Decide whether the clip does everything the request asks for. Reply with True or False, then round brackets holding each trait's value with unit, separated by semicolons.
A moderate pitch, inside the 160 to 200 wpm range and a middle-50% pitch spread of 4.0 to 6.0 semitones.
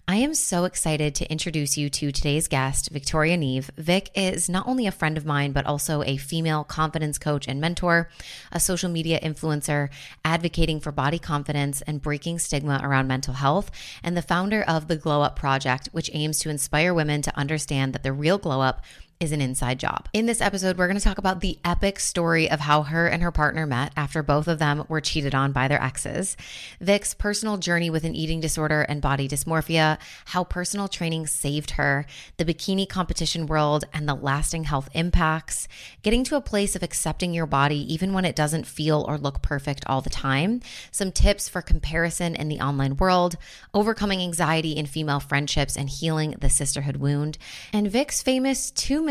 False (155 Hz; 195 wpm; 3.3 semitones)